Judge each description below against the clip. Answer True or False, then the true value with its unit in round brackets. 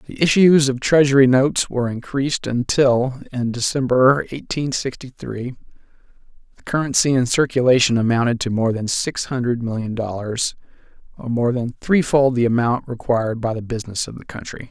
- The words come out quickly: False (155 wpm)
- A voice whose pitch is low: True (125 Hz)